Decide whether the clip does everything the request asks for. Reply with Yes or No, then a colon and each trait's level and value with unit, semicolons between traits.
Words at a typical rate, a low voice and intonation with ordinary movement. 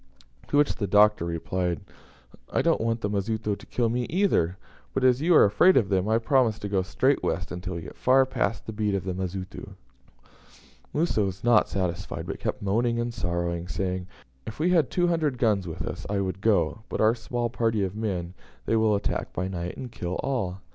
No: fast, 210 wpm; low, 105 Hz; average, 4.5 semitones